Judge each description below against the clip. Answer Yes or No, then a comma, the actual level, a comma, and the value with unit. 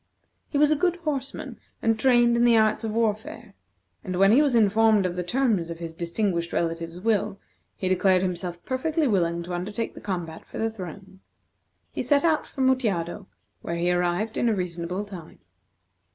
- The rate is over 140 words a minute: Yes, average, 180 wpm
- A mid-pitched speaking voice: No, high, 200 Hz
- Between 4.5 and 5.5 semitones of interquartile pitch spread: Yes, average, 5.1 semitones